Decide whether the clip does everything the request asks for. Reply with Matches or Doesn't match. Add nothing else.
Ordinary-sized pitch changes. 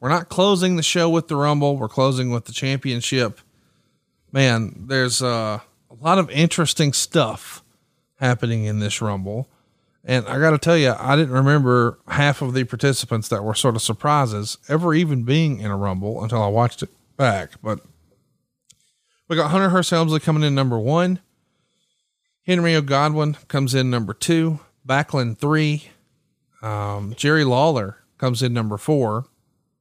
Matches